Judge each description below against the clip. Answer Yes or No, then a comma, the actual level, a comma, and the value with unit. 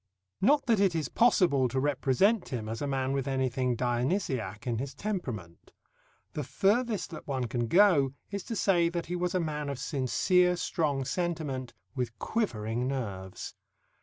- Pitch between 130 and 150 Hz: Yes, medium, 140 Hz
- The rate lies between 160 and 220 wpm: Yes, average, 165 wpm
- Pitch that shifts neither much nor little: No, wide, 6.1 semitones